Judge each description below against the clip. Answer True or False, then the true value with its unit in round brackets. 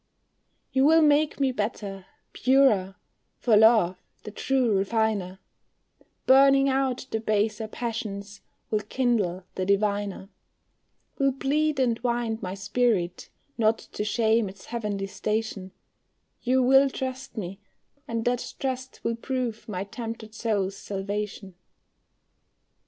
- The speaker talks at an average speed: False (120 wpm)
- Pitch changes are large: False (4.3 semitones)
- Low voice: False (220 Hz)